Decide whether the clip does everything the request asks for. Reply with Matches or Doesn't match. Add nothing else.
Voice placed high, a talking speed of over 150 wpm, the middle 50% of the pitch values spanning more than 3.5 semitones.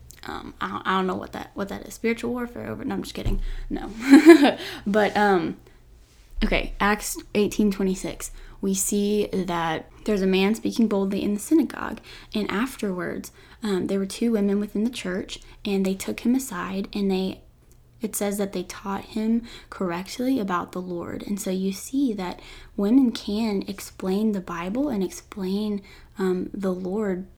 Doesn't match